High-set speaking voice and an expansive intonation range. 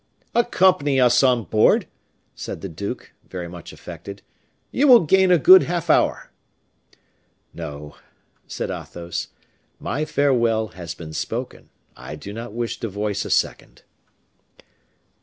No: low, 115 Hz; wide, 8.7 semitones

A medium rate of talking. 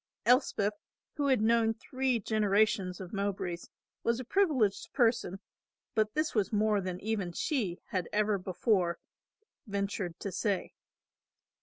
No: slow, 130 wpm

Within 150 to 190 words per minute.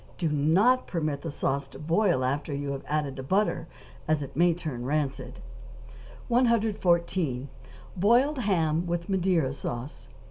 No: average, 140 wpm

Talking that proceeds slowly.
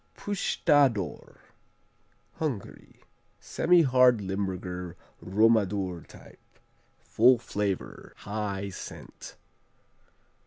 Yes: slow, 55 wpm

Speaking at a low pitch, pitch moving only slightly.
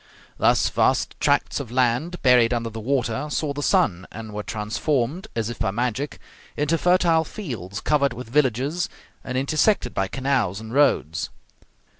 No: low, 125 Hz; average, 4.9 semitones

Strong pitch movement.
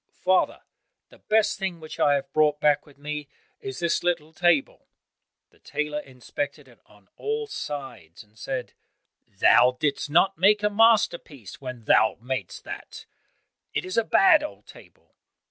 Yes: wide, 6.3 semitones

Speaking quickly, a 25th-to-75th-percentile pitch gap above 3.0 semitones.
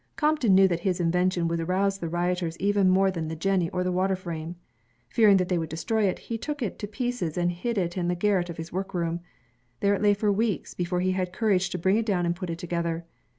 No: fast, 245 wpm; narrow, 2.5 semitones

